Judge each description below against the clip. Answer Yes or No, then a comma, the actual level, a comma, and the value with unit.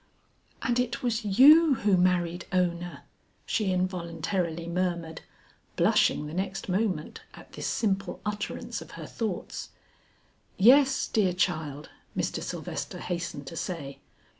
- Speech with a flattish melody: No, average, 3.8 semitones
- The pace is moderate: No, slow, 120 wpm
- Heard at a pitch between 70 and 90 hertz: No, medium, 185 Hz